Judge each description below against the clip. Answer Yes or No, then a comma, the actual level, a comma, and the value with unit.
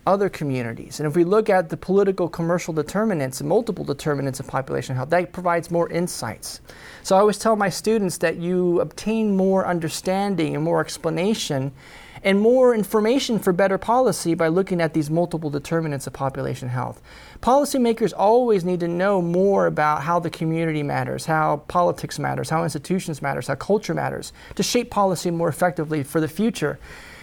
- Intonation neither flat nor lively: Yes, average, 4.0 semitones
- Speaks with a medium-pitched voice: Yes, medium, 175 Hz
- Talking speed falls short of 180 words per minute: Yes, average, 170 wpm